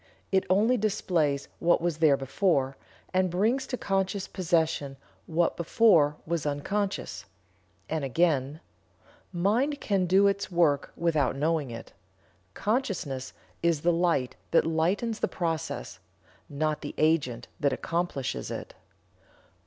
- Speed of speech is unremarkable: No, slow, 120 wpm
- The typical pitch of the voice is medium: Yes, medium, 170 Hz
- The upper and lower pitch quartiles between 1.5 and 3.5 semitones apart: No, average, 4.9 semitones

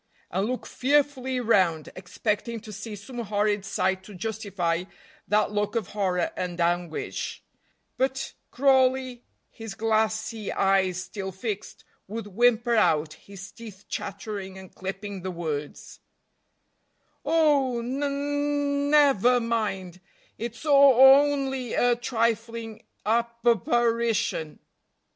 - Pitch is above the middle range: Yes, high, 220 Hz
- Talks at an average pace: No, slow, 115 wpm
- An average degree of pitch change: Yes, average, 4.5 semitones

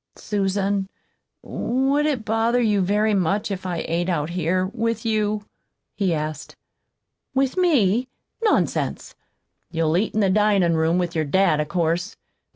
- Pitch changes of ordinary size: Yes, average, 4.2 semitones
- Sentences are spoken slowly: No, average, 145 wpm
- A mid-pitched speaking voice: No, high, 195 Hz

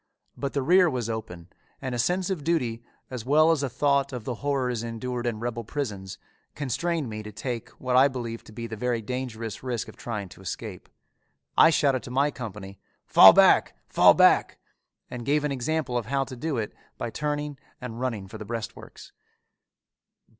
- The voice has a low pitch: Yes, low, 125 Hz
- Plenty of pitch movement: No, average, 3.6 semitones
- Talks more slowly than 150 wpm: No, average, 190 wpm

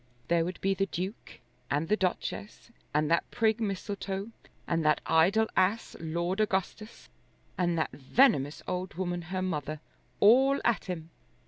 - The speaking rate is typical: Yes, average, 145 wpm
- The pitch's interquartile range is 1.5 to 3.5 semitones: No, average, 4.0 semitones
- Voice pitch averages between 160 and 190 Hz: Yes, medium, 185 Hz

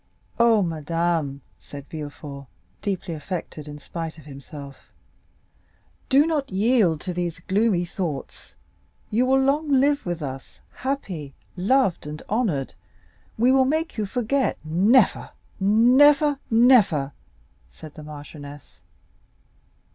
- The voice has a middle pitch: Yes, medium, 180 Hz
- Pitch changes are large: Yes, wide, 8.8 semitones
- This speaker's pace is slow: Yes, slow, 115 wpm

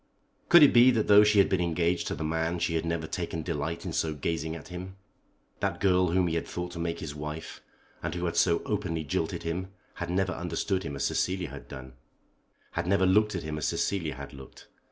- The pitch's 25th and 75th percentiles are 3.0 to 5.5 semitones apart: No, narrow, 2.6 semitones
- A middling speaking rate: No, fast, 225 wpm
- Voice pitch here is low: Yes, very low, 85 Hz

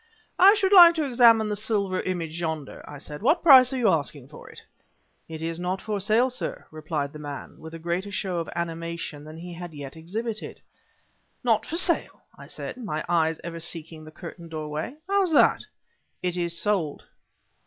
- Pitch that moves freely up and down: Yes, wide, 5.9 semitones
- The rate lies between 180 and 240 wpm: Yes, average, 185 wpm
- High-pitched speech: No, medium, 175 Hz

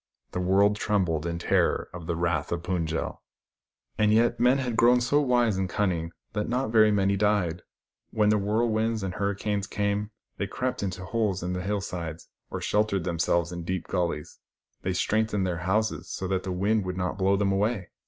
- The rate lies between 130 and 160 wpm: No, average, 200 wpm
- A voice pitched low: Yes, low, 100 Hz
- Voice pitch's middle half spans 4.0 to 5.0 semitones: No, average, 3.1 semitones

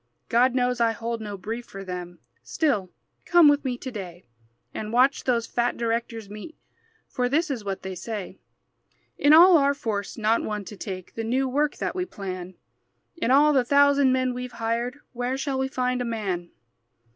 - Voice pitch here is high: Yes, high, 240 Hz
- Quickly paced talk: No, average, 185 wpm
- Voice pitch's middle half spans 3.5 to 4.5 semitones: Yes, average, 4.2 semitones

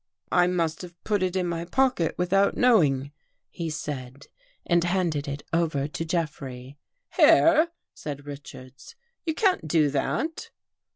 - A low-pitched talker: No, medium, 165 Hz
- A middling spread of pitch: Yes, average, 4.2 semitones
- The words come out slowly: No, average, 150 wpm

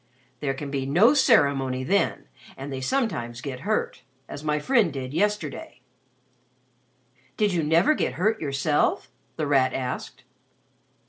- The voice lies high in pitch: No, medium, 145 Hz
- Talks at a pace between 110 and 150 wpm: Yes, slow, 135 wpm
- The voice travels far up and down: Yes, wide, 7.0 semitones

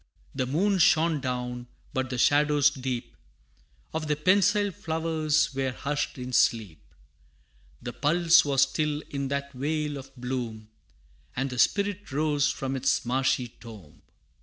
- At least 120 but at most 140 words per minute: Yes, slow, 135 wpm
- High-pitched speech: No, medium, 140 Hz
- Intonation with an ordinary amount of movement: Yes, average, 3.4 semitones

